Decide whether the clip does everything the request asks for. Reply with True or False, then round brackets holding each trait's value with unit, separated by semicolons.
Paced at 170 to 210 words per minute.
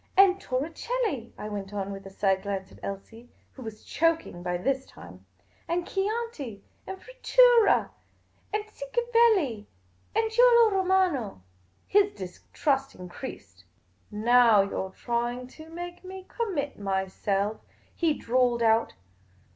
False (140 wpm)